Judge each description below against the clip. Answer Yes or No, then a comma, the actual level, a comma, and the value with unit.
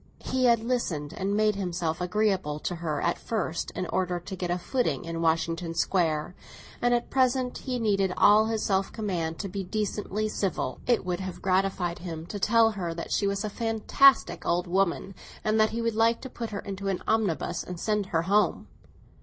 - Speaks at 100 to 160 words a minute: No, average, 195 wpm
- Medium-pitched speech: No, high, 195 Hz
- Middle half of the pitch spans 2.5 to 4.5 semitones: Yes, average, 3.9 semitones